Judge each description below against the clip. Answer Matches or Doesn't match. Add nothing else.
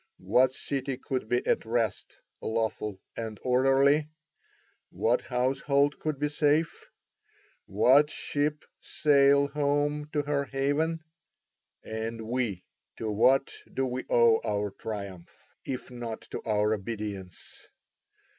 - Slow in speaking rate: Matches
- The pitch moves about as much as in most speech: Matches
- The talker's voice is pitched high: Doesn't match